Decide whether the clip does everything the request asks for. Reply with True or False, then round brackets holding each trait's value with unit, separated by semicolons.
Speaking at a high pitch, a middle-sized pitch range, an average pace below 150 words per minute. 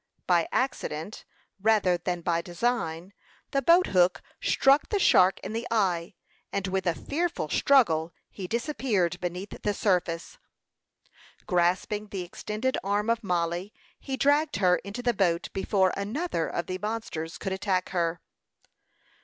True (195 Hz; 4.6 semitones; 140 wpm)